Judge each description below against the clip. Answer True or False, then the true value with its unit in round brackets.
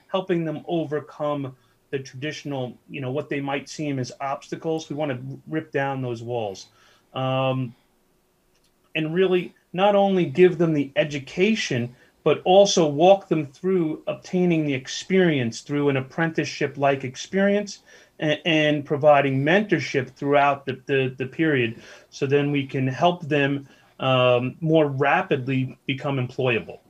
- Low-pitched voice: False (145 Hz)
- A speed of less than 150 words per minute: True (140 wpm)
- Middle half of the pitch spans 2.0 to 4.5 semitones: True (3.8 semitones)